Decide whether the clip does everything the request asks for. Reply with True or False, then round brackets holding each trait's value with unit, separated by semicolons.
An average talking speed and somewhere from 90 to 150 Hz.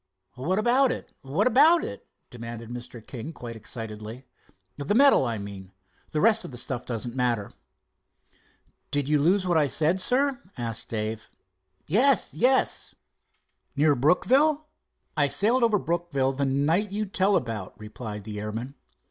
True (145 wpm; 140 Hz)